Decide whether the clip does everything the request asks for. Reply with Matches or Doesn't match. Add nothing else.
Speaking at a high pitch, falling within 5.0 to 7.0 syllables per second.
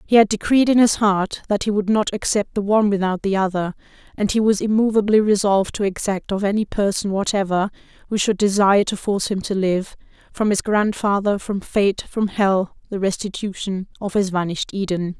Matches